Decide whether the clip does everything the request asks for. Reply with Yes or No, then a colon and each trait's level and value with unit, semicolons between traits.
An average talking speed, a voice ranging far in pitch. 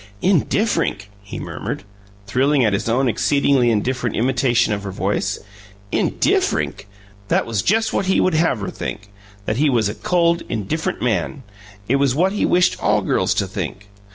Yes: average, 165 wpm; wide, 7.2 semitones